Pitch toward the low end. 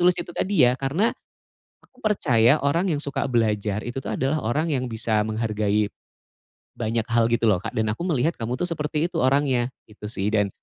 Yes: low, 125 Hz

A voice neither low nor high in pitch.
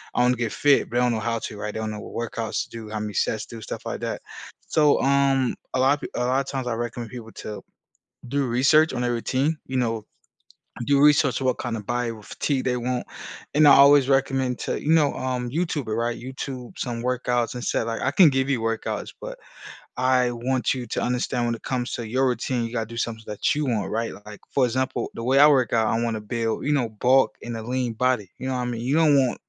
No: low, 125 Hz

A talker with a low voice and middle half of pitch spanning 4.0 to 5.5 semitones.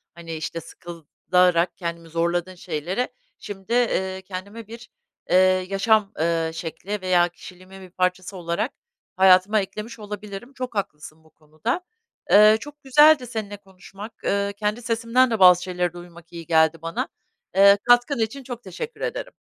No: high, 190 Hz; average, 4.3 semitones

